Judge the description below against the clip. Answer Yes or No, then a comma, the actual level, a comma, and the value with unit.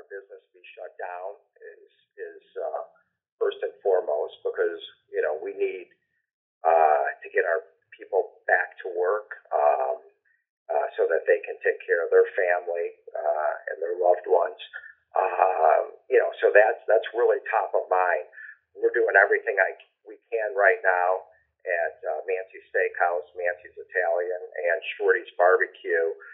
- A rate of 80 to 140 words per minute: No, average, 150 wpm